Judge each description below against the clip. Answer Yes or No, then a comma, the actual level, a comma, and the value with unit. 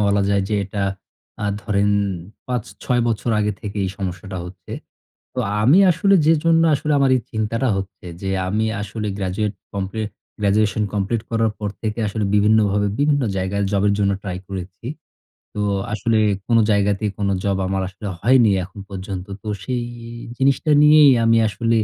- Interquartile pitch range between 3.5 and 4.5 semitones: No, average, 2.9 semitones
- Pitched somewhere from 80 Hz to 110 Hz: Yes, low, 105 Hz